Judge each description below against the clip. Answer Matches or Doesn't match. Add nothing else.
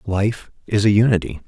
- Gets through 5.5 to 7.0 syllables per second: Doesn't match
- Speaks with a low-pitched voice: Matches